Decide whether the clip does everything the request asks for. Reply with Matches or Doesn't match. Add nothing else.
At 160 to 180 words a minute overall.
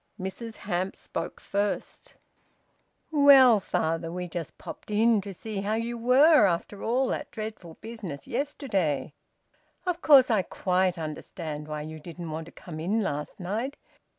Doesn't match